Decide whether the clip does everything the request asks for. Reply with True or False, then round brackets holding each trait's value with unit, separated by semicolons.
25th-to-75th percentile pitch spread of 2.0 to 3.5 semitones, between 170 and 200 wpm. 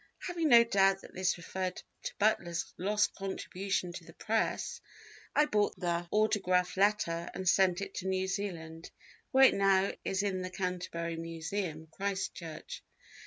False (2.7 semitones; 150 wpm)